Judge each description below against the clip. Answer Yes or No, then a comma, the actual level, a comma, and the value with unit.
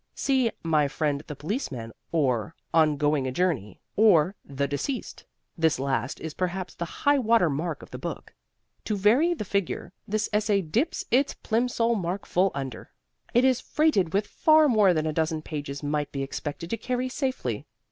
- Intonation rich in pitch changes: Yes, wide, 7.5 semitones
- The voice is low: No, medium, 175 Hz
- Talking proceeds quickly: No, average, 175 wpm